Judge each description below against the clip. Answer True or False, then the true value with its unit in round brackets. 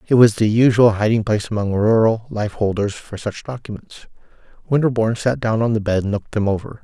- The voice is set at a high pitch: False (110 Hz)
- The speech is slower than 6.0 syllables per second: False (6.2 syllables/s)